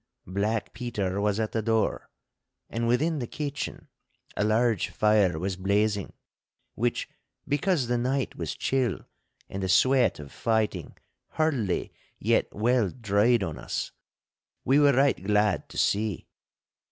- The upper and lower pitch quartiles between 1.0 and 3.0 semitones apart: No, average, 3.7 semitones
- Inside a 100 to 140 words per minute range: Yes, slow, 135 wpm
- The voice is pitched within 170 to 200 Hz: No, low, 110 Hz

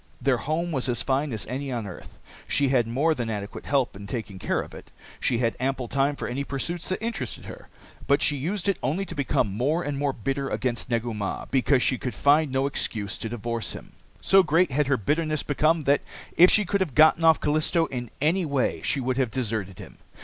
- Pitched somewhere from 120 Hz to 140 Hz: Yes, low, 135 Hz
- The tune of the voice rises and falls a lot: No, average, 4.4 semitones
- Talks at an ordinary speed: No, fast, 220 wpm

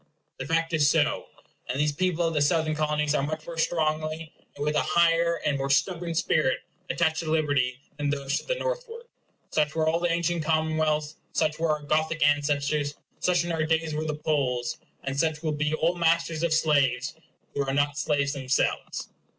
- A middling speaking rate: Yes, average, 190 wpm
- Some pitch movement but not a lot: No, narrow, 2.2 semitones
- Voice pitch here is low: No, medium, 155 Hz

